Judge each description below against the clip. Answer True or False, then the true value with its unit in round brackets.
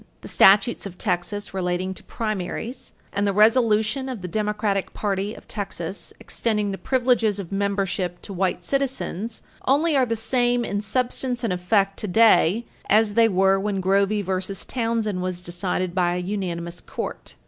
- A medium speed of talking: True (160 wpm)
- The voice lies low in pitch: False (205 Hz)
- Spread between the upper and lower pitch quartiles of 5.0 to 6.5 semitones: False (3.5 semitones)